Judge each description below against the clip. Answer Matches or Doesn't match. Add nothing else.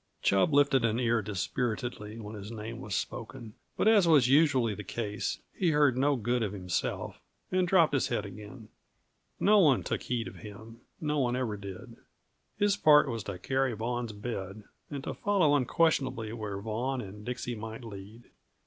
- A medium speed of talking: Matches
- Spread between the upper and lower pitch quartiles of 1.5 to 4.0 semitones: Doesn't match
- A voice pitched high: Doesn't match